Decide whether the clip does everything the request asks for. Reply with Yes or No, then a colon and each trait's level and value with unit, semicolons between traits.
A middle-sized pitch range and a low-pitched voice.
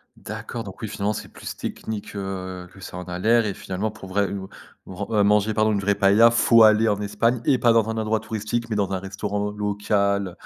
No: narrow, 2.0 semitones; low, 105 Hz